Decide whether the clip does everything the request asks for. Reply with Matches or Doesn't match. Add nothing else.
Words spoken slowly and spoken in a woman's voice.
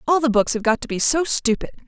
Doesn't match